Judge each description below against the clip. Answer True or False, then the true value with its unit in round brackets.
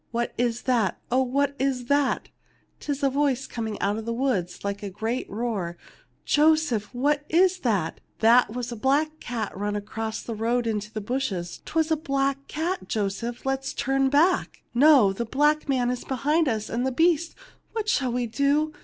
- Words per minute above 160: True (190 wpm)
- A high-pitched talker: True (250 Hz)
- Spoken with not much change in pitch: False (4.3 semitones)